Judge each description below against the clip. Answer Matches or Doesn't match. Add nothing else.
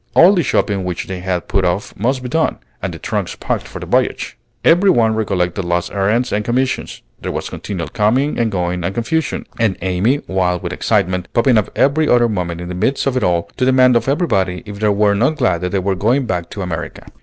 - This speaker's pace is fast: Matches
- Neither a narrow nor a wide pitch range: Doesn't match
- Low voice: Matches